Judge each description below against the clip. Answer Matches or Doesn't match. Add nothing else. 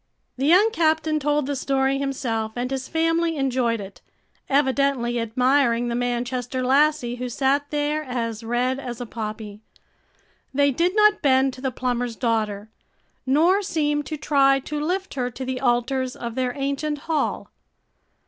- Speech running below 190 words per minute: Matches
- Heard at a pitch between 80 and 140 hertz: Doesn't match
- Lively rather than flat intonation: Doesn't match